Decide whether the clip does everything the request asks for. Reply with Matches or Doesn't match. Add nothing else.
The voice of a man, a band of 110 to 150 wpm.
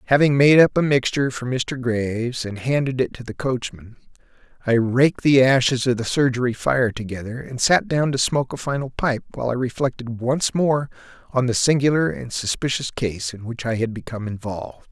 Doesn't match